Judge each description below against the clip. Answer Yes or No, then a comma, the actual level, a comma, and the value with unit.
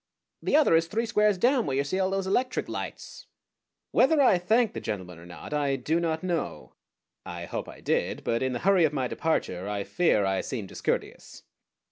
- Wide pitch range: Yes, wide, 9.0 semitones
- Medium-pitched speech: Yes, medium, 160 Hz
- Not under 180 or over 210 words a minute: Yes, average, 200 wpm